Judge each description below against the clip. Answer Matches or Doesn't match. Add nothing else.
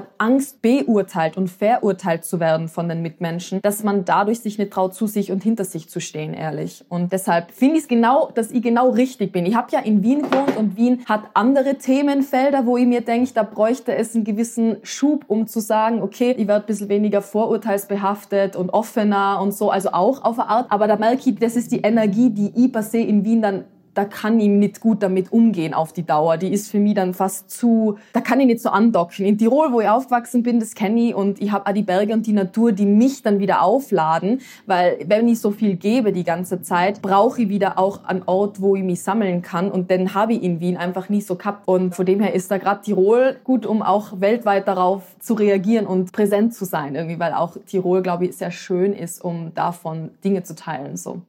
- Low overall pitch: Doesn't match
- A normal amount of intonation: Matches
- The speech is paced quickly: Matches